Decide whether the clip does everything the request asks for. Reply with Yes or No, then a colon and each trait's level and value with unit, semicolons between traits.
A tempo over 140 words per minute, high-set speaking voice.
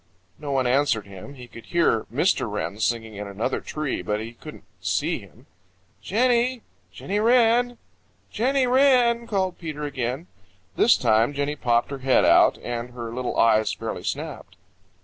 No: average, 155 wpm; medium, 140 Hz